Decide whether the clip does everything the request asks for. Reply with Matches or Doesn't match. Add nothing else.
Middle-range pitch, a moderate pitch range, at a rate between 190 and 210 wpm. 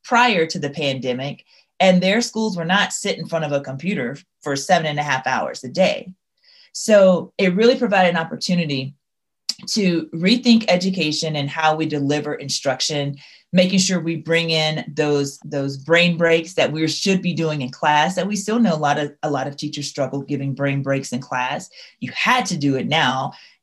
Matches